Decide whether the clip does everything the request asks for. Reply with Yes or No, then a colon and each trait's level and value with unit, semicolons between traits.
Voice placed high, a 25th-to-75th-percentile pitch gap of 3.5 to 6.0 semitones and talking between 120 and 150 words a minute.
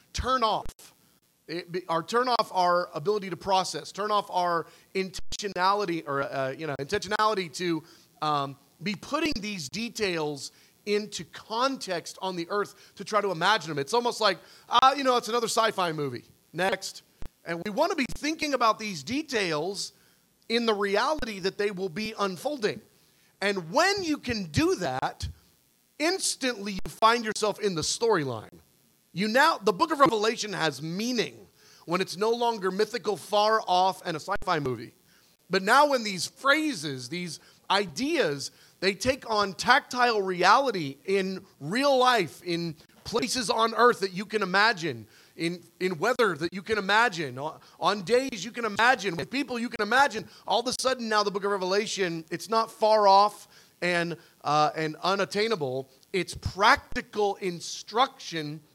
No: high, 200 Hz; average, 4.6 semitones; average, 160 wpm